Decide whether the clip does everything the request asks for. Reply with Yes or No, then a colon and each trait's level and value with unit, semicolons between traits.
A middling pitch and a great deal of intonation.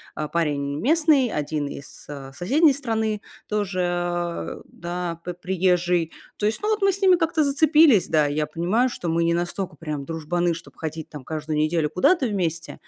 Yes: medium, 175 Hz; wide, 6.1 semitones